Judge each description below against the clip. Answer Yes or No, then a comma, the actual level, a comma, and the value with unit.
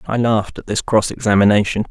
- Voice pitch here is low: Yes, low, 110 Hz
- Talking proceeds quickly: No, average, 190 wpm